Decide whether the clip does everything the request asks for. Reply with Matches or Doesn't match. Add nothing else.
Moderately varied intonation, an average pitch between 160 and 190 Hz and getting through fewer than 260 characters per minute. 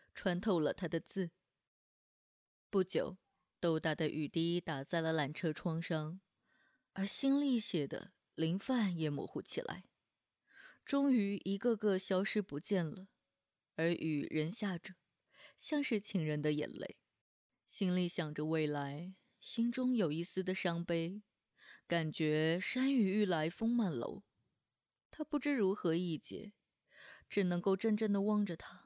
Matches